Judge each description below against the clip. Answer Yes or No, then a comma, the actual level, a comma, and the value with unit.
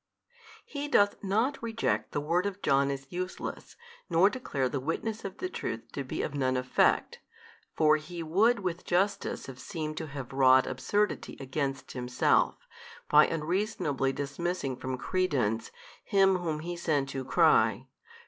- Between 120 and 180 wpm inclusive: Yes, average, 155 wpm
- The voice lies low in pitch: No, medium, 155 Hz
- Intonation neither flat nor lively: No, wide, 5.9 semitones